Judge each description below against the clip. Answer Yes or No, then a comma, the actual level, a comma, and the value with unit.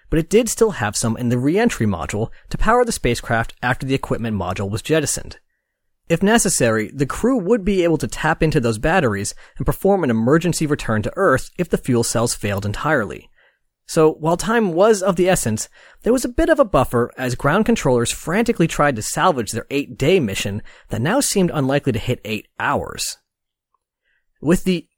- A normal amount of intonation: No, wide, 8.3 semitones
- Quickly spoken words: No, average, 195 wpm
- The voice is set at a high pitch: No, medium, 145 Hz